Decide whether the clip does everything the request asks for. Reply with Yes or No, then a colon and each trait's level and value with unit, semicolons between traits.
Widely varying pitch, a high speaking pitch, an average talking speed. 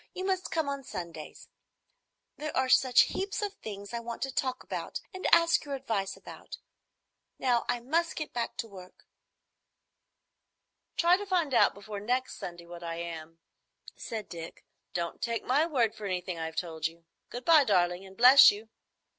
Yes: wide, 7.8 semitones; high, 230 Hz; average, 170 wpm